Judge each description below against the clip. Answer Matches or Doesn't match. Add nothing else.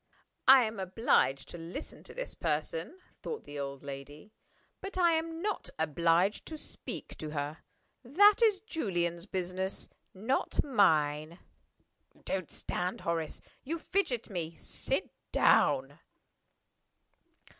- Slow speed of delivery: Matches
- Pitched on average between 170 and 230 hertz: Matches